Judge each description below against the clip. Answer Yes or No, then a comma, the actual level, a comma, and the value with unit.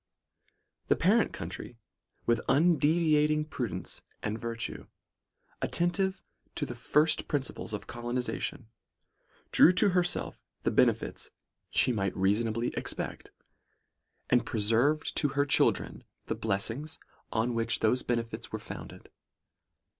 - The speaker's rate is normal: No, slow, 115 wpm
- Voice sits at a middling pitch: No, low, 125 Hz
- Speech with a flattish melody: No, average, 5.0 semitones